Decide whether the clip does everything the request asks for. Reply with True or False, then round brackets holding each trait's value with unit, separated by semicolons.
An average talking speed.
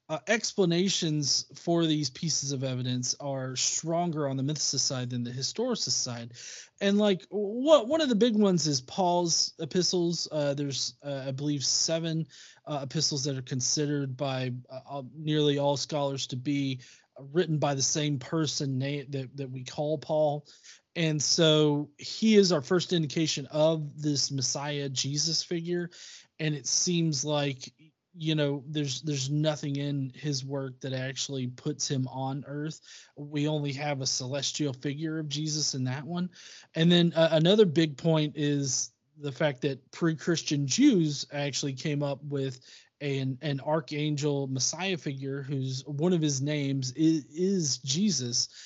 True (155 wpm)